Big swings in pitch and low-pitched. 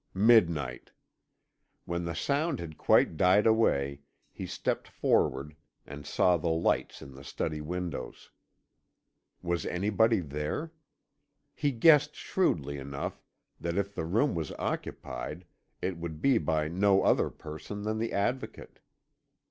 Yes: wide, 6.0 semitones; very low, 85 Hz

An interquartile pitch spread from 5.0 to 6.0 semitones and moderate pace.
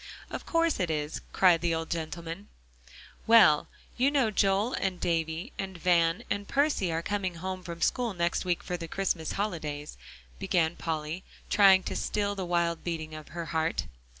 No: average, 3.3 semitones; average, 170 wpm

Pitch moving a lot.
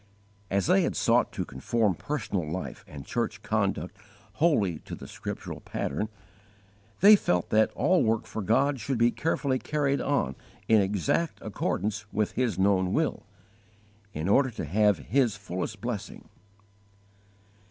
Yes: wide, 5.8 semitones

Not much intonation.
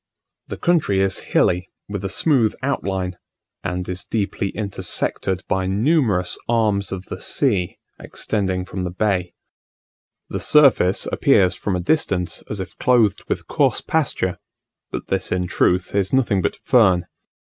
No: average, 3.5 semitones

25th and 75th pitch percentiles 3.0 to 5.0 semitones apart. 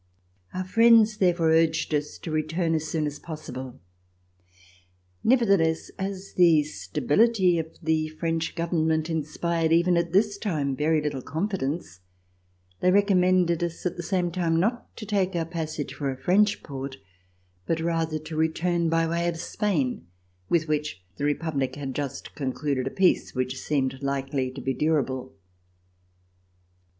Yes: average, 3.4 semitones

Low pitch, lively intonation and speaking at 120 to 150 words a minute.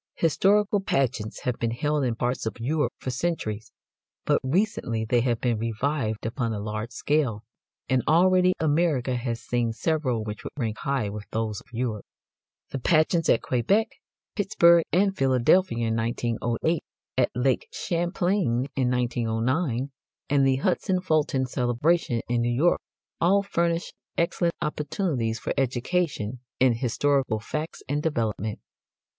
Yes: low, 130 Hz; wide, 5.9 semitones; average, 140 wpm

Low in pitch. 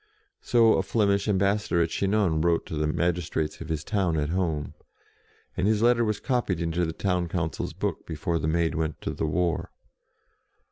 Yes: very low, 85 Hz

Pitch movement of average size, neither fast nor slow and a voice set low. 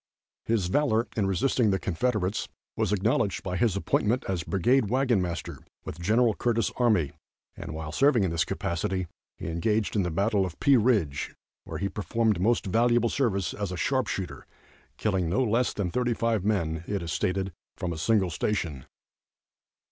Yes: average, 4.5 semitones; average, 170 wpm; low, 100 Hz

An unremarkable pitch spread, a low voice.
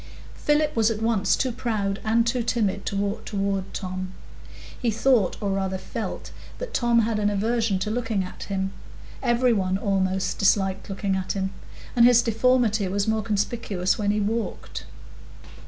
No: average, 3.1 semitones; high, 210 Hz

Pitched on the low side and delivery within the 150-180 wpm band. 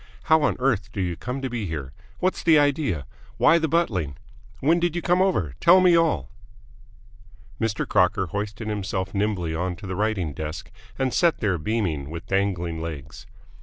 Yes: low, 105 Hz; average, 170 wpm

